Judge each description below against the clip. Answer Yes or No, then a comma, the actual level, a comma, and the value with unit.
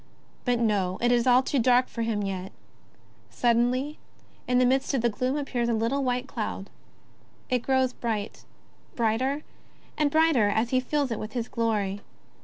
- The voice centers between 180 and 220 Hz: No, high, 245 Hz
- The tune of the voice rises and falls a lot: No, average, 2.7 semitones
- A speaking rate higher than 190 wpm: No, average, 170 wpm